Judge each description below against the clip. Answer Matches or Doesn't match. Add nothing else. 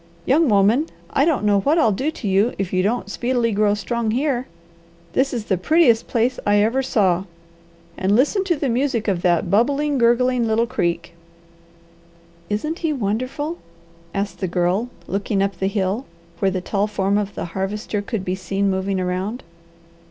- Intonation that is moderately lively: Matches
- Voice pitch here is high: Matches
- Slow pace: Doesn't match